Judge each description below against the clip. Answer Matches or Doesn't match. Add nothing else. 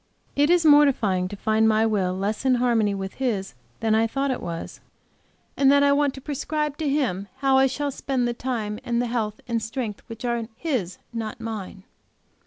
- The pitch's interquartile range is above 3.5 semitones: Matches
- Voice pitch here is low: Doesn't match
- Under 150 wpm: Doesn't match